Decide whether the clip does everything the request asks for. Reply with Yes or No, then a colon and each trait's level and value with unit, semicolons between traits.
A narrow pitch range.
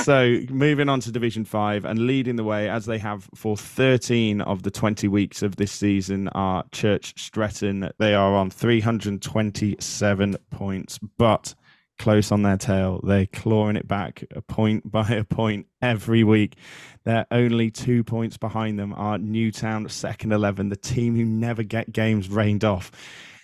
Yes: narrow, 2.1 semitones